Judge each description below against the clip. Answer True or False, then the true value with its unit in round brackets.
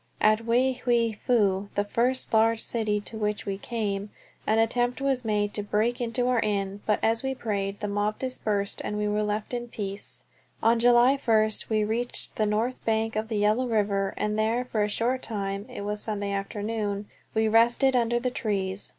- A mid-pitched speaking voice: False (220 Hz)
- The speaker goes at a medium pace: True (195 wpm)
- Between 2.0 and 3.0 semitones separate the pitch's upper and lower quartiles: True (2.4 semitones)